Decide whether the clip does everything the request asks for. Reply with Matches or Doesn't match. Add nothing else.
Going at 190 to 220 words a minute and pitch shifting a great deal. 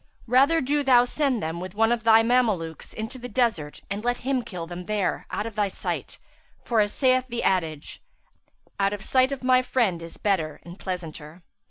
Matches